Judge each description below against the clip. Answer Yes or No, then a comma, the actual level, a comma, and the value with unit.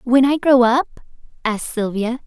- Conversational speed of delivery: Yes, average, 160 wpm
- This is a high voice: Yes, very high, 250 Hz